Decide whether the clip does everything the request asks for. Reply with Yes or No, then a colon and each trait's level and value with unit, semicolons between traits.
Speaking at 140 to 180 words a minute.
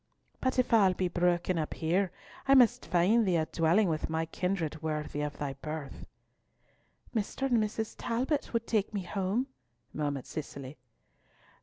Yes: average, 155 wpm